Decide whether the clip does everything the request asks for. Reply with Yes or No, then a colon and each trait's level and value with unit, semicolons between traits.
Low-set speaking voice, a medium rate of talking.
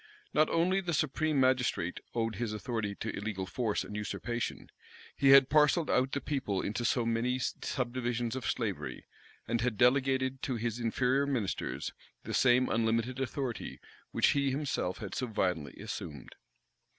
Yes: low, 125 Hz; average, 150 wpm